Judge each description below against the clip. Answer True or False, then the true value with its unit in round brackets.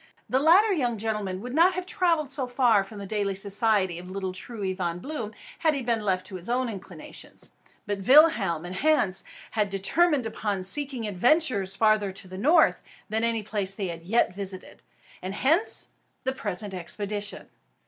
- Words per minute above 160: True (170 wpm)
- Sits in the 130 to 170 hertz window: False (210 Hz)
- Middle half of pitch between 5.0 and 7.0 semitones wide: True (5.4 semitones)